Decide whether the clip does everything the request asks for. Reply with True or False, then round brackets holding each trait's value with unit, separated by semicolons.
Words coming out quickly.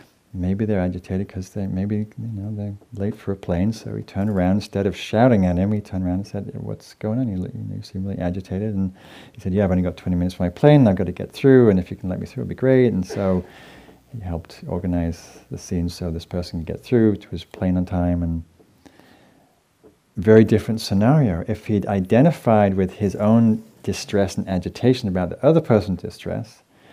True (220 wpm)